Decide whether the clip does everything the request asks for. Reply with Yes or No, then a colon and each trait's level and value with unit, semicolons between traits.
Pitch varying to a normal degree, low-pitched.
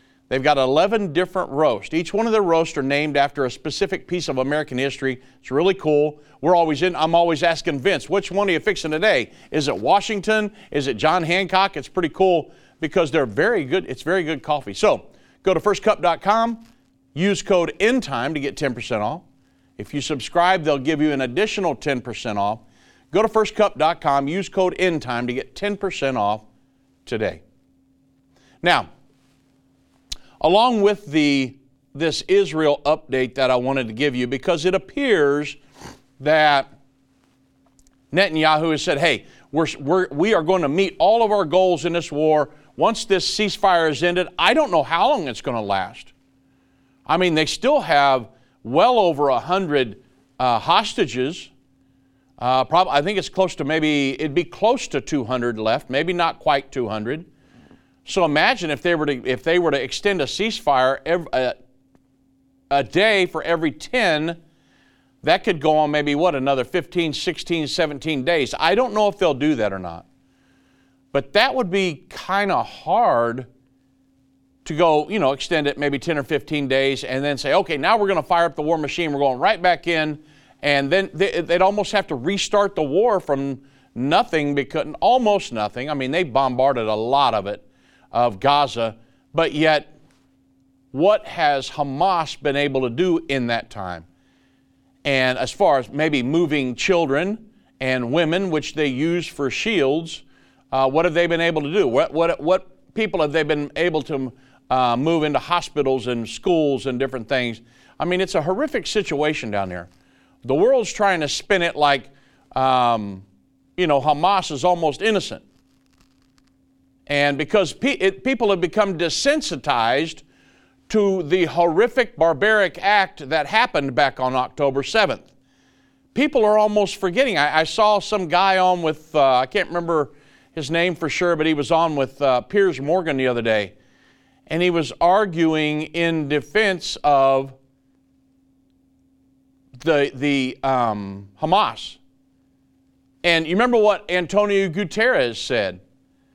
No: average, 5.0 semitones; medium, 150 Hz